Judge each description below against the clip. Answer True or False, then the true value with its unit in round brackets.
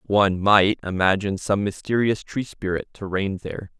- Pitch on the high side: False (100 Hz)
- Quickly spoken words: False (160 wpm)